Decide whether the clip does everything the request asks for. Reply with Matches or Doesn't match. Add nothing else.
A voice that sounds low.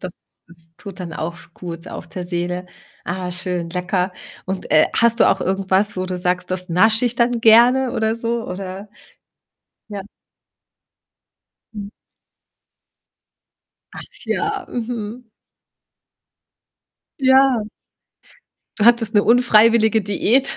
Doesn't match